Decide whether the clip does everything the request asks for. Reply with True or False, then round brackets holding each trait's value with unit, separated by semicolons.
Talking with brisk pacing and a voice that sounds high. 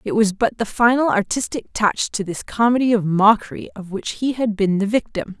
True (210 wpm; 215 Hz)